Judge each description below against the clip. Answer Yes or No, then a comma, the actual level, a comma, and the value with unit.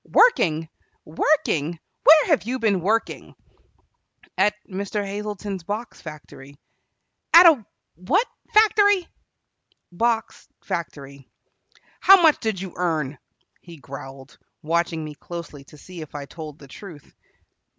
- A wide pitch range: Yes, wide, 6.8 semitones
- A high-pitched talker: No, medium, 180 Hz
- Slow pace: Yes, slow, 120 wpm